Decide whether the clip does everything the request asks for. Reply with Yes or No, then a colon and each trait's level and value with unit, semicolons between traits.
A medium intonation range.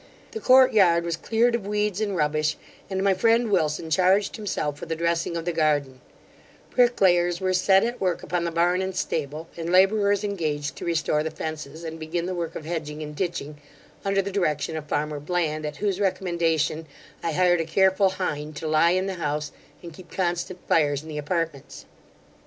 Yes: average, 3.6 semitones